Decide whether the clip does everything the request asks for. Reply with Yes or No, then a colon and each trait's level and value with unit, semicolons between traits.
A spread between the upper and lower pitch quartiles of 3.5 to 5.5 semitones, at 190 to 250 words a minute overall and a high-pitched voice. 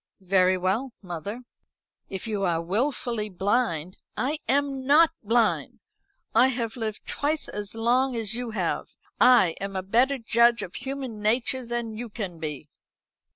No: average, 4.4 semitones; average, 155 wpm; high, 230 Hz